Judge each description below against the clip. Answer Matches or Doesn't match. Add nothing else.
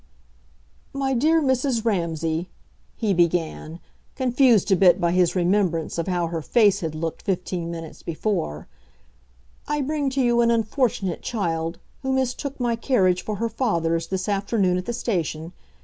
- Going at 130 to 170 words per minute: Matches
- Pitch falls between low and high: Doesn't match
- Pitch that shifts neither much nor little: Doesn't match